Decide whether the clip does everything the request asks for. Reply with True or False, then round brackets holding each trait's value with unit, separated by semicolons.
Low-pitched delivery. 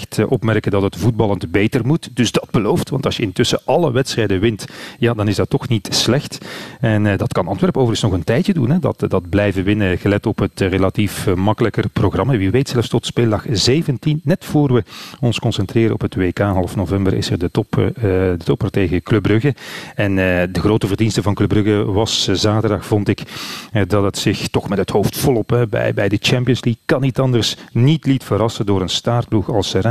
True (110 Hz)